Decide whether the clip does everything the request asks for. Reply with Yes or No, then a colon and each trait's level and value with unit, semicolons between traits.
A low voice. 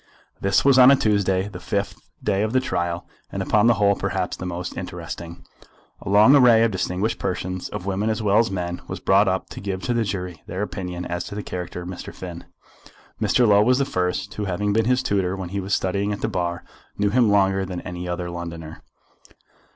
Yes: very low, 95 Hz